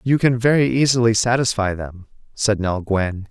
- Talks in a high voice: No, low, 110 Hz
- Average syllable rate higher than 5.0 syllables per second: No, 4.8 syllables/s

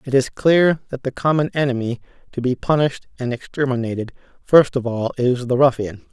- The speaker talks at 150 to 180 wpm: Yes, average, 175 wpm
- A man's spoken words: Yes, male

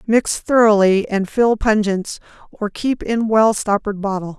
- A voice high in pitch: Yes, high, 210 Hz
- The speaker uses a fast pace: No, average, 150 wpm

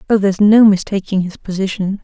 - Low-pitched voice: No, high, 195 Hz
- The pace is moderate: Yes, average, 175 wpm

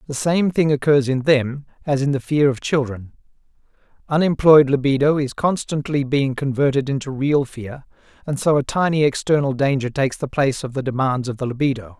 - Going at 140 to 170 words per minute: No, average, 180 wpm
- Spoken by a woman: No, male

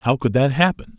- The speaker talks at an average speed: No, fast, 245 wpm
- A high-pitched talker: No, low, 135 Hz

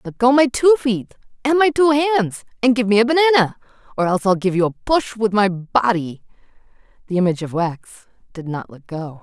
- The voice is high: Yes, high, 220 Hz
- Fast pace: Yes, fast, 210 wpm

